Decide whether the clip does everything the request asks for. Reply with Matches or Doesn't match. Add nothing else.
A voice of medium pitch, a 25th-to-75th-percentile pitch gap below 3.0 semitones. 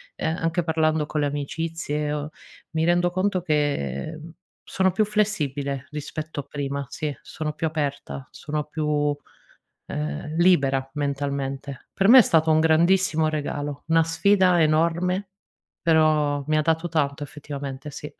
Matches